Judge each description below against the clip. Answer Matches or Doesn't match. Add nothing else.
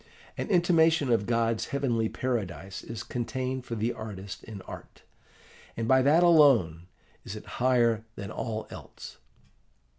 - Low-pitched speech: Matches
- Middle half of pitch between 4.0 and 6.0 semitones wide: Doesn't match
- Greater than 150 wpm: Doesn't match